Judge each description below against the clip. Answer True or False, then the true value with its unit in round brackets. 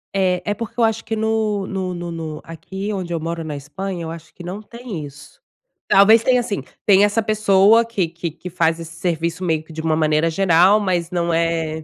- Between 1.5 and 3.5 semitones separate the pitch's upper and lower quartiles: False (3.9 semitones)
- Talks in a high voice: False (180 Hz)